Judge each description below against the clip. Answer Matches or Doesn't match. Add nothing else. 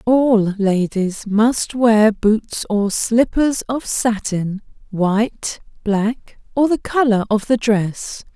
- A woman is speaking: Matches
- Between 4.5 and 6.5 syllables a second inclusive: Doesn't match